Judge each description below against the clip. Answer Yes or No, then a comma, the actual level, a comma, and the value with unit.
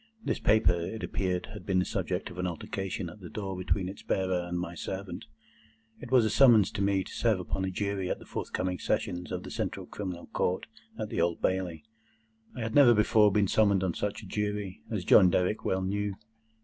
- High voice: No, very low, 95 Hz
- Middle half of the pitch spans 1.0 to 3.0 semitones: Yes, narrow, 2.4 semitones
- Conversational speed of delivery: No, fast, 215 wpm